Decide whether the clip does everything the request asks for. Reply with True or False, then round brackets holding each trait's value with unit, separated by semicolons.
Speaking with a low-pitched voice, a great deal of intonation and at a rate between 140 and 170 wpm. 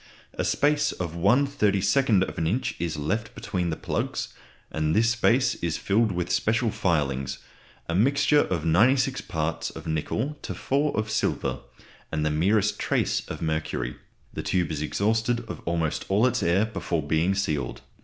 True (95 Hz; 6.5 semitones; 155 wpm)